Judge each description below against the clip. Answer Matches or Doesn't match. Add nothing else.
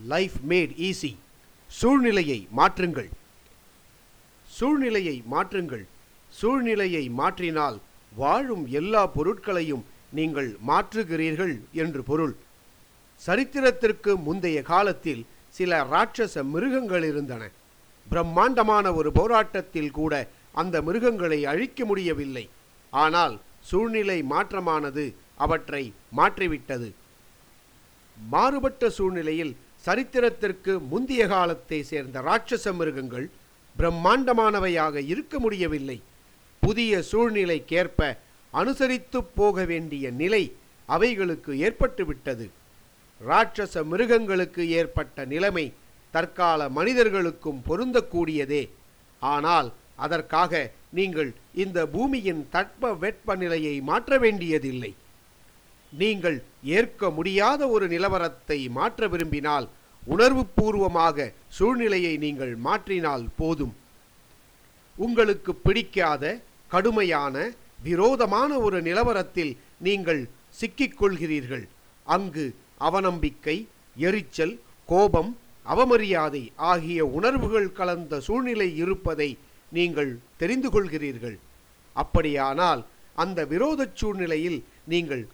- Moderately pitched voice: Matches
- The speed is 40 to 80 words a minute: Matches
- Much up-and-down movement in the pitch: Matches